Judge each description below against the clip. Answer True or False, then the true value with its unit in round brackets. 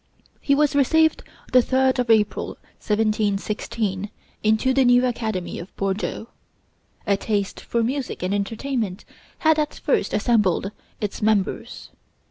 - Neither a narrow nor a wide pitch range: True (4.2 semitones)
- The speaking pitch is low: False (220 Hz)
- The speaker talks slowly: True (125 wpm)